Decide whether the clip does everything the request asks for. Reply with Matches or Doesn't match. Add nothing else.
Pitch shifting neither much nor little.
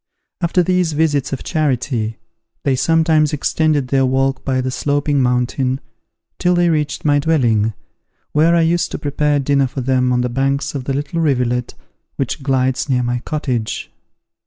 Matches